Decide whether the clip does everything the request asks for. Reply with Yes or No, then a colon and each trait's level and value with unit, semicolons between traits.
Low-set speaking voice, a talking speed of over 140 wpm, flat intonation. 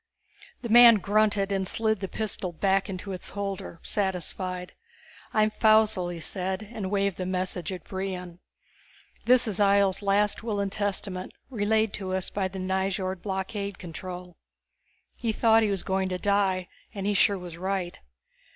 No: high, 195 Hz; average, 160 wpm; narrow, 1.9 semitones